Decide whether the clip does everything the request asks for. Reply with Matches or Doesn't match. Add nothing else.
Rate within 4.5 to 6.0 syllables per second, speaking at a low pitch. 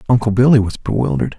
Doesn't match